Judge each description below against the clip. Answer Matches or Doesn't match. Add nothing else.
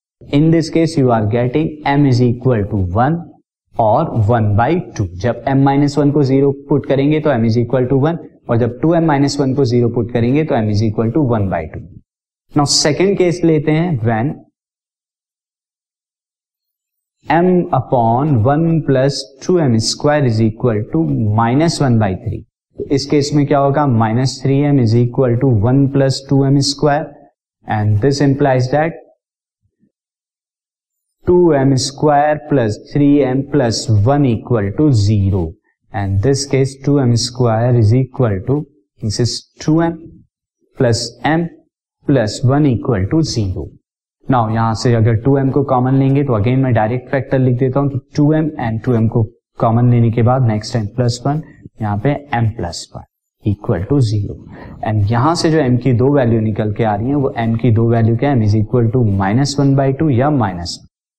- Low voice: Matches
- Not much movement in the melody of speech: Doesn't match